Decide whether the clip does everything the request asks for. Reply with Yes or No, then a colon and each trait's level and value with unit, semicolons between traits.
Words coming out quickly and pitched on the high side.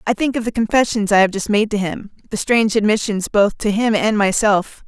Yes: fast, 235 wpm; high, 215 Hz